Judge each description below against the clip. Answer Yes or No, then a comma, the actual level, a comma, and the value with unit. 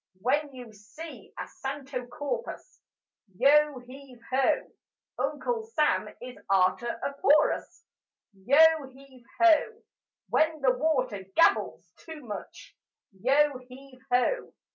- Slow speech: Yes, slow, 110 wpm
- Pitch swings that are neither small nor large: Yes, average, 3.5 semitones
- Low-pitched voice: No, very high, 270 Hz